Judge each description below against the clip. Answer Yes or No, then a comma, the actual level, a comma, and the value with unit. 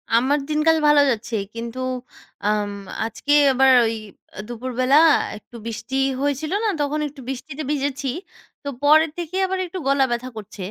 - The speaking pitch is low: No, very high, 270 Hz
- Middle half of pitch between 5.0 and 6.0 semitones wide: No, average, 4.1 semitones